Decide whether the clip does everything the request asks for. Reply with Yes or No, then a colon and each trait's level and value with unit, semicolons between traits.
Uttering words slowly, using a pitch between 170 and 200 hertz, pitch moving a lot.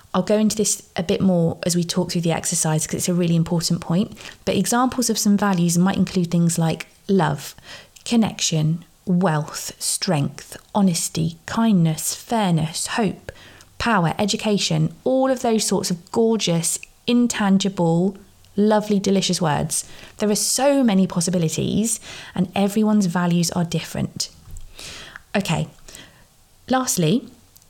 No: slow, 130 wpm; high, 190 Hz; average, 3.6 semitones